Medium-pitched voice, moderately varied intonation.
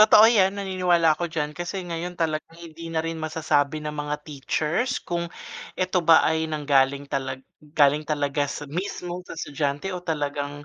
Yes: medium, 160 Hz; average, 3.1 semitones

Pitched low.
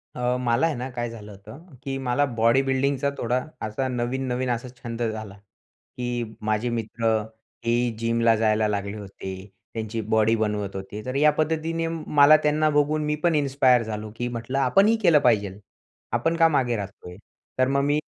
Yes: low, 120 Hz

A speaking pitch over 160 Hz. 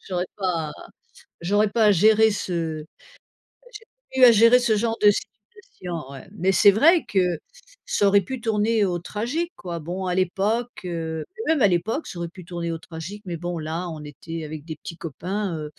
Yes: medium, 185 Hz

